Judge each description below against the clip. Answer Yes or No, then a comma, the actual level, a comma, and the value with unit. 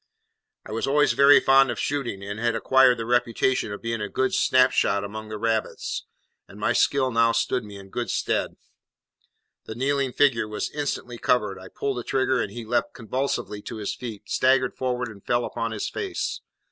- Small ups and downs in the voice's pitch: No, average, 3.3 semitones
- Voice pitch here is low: Yes, low, 120 Hz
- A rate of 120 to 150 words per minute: No, average, 195 wpm